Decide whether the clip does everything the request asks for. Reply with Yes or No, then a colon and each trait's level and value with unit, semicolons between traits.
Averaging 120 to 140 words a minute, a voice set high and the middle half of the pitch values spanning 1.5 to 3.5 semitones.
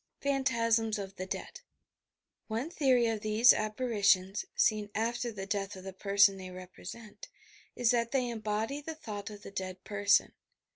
No: average, 155 wpm; high, 215 Hz; average, 3.0 semitones